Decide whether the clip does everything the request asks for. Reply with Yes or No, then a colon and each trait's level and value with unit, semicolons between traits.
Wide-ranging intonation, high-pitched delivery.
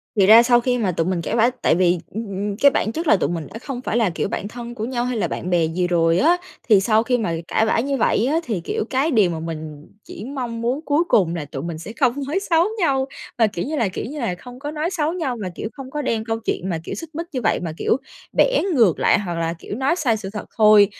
Yes: wide, 6.5 semitones; high, 225 Hz